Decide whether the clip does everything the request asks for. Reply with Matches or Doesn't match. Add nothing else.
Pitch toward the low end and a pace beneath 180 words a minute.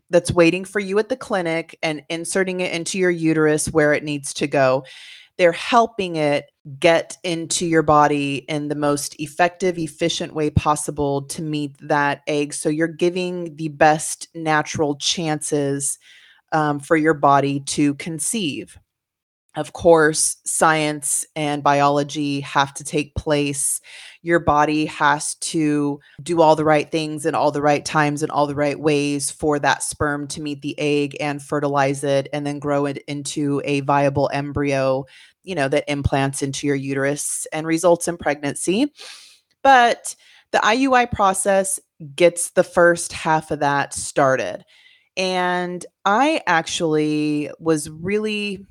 Doesn't match